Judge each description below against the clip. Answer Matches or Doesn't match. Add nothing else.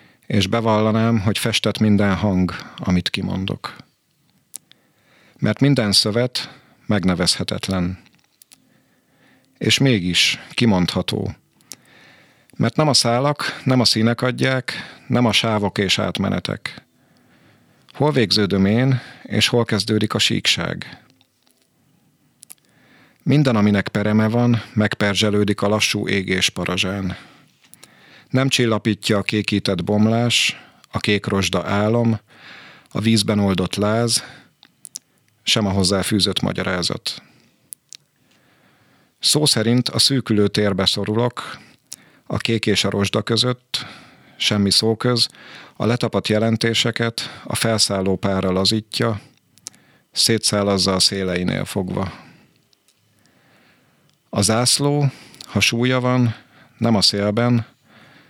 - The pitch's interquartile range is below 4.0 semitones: Matches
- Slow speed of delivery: Matches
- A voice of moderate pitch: Doesn't match